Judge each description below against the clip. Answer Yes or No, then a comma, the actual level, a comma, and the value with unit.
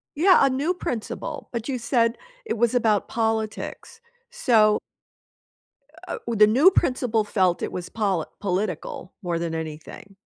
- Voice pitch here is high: Yes, high, 220 Hz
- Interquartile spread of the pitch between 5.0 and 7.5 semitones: No, average, 4.5 semitones